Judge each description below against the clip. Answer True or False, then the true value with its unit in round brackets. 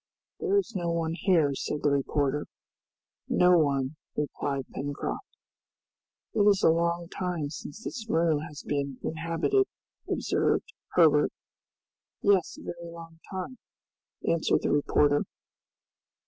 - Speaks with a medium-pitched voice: True (165 Hz)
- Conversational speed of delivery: False (120 wpm)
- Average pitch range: True (3.8 semitones)